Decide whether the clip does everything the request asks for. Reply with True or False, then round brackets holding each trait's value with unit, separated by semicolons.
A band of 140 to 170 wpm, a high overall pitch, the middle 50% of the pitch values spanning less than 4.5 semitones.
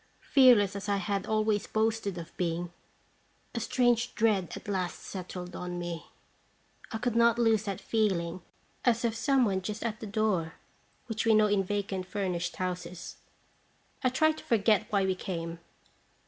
True (165 wpm; 205 Hz; 3.6 semitones)